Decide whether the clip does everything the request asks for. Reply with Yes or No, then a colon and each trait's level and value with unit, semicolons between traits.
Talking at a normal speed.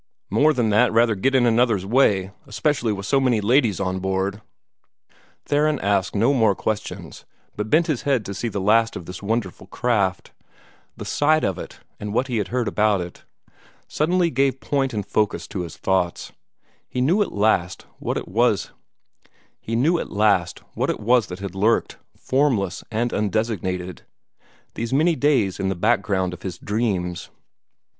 Yes: average, 160 wpm